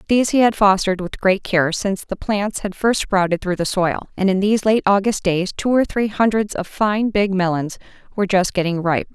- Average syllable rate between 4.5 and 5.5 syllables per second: Yes, 5.4 syllables/s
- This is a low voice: No, high, 195 Hz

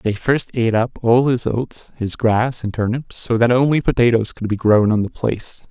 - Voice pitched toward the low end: Yes, low, 115 Hz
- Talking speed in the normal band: No, fast, 220 wpm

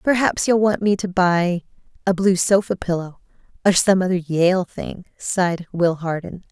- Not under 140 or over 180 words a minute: Yes, average, 165 wpm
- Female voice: Yes, female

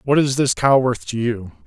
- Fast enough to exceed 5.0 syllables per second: No, 4.9 syllables/s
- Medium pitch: No, low, 125 Hz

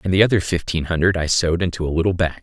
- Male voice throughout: Yes, male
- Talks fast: Yes, fast, 270 wpm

